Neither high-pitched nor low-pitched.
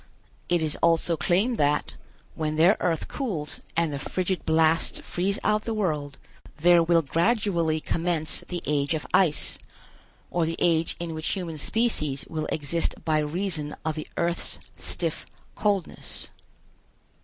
Yes: medium, 165 Hz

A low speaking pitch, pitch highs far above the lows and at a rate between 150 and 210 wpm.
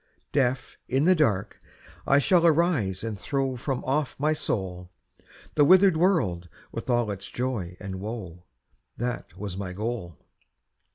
No: low, 120 Hz; wide, 7.3 semitones; average, 140 wpm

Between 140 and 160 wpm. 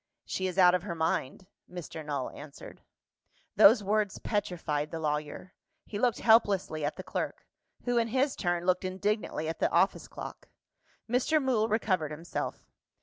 Yes: average, 155 wpm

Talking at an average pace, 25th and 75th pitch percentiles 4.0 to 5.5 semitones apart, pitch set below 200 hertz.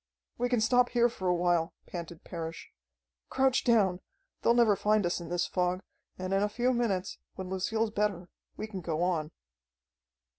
Yes: average, 175 wpm; average, 4.3 semitones; high, 190 Hz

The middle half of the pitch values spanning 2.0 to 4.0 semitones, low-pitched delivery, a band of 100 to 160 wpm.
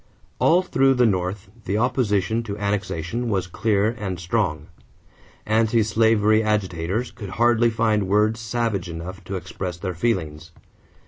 Yes: average, 3.5 semitones; low, 105 Hz; average, 140 wpm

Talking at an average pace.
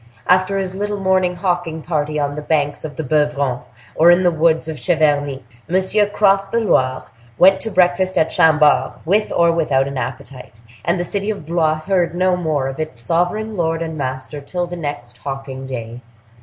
Yes: average, 185 wpm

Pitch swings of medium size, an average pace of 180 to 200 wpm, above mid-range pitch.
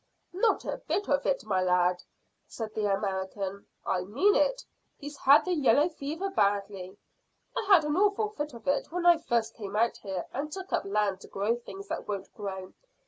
No: wide, 7.8 semitones; average, 195 wpm; high, 230 Hz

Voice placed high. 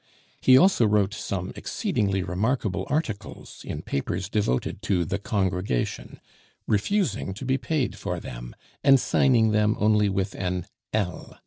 No: low, 105 Hz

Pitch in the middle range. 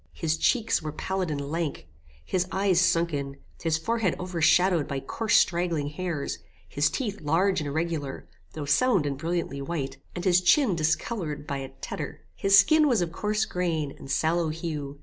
Yes: medium, 165 Hz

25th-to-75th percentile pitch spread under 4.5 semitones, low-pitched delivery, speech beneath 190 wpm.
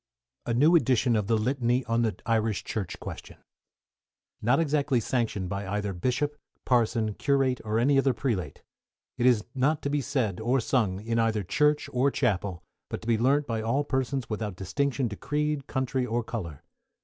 Yes: average, 3.9 semitones; low, 120 Hz; average, 175 wpm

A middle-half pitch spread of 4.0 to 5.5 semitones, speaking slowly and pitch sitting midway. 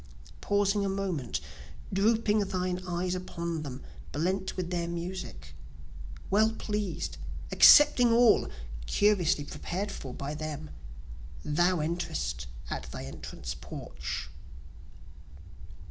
Yes: average, 4.4 semitones; slow, 100 wpm; medium, 180 Hz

